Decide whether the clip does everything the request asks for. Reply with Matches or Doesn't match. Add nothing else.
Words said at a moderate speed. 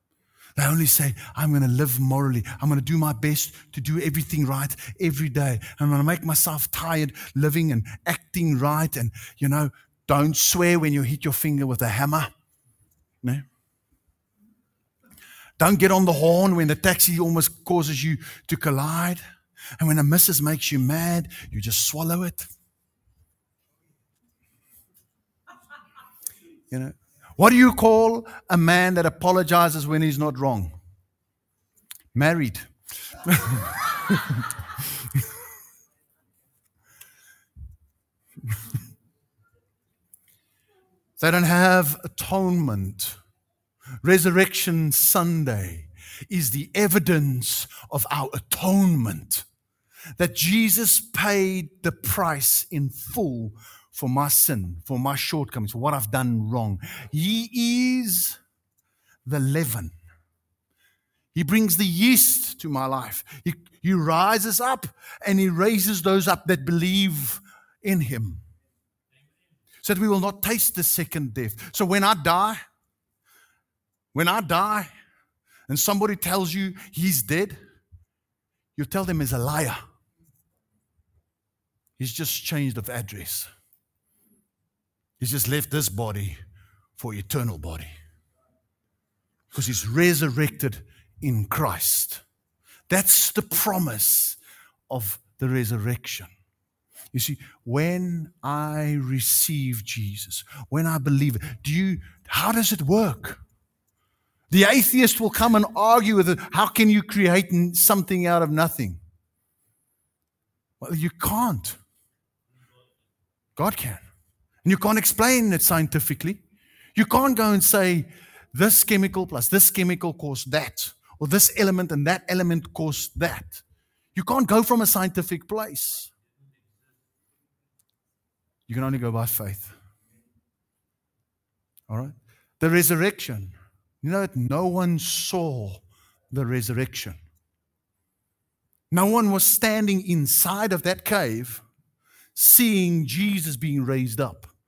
Doesn't match